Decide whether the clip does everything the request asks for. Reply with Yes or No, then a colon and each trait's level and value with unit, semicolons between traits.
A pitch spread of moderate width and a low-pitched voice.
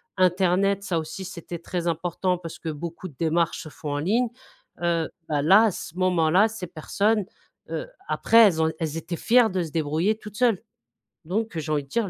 No: average, 3.7 semitones; medium, 175 Hz